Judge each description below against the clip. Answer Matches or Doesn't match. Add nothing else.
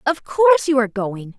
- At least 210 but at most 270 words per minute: Matches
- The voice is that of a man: Doesn't match